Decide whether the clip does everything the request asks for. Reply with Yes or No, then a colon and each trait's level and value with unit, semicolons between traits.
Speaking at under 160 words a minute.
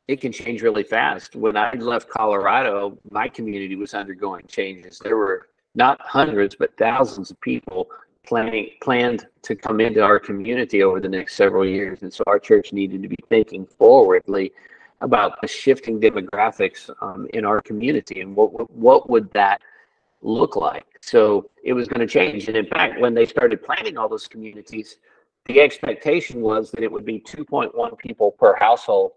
No: average, 180 wpm